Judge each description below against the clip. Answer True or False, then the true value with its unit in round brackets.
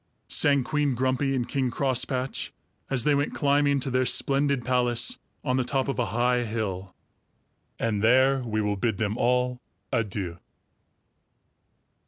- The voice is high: False (125 Hz)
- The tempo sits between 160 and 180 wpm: False (145 wpm)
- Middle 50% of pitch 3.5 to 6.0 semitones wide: False (3.0 semitones)